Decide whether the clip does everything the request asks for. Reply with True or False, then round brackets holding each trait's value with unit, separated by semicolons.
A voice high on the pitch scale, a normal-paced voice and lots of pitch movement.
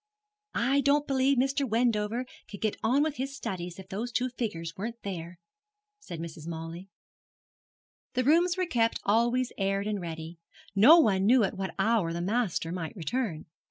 True (215 Hz; 165 wpm; 6.0 semitones)